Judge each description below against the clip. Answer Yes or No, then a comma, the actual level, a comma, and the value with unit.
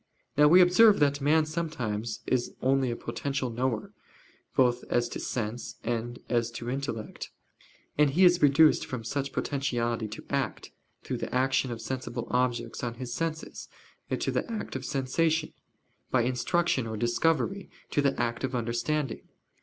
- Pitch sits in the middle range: No, low, 130 Hz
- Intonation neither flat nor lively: Yes, average, 4.0 semitones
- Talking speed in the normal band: Yes, average, 155 wpm